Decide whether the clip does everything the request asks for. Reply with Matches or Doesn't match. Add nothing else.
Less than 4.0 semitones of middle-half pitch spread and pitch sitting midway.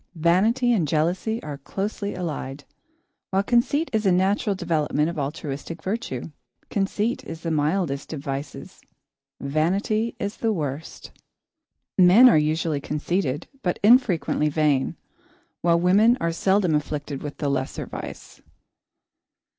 Doesn't match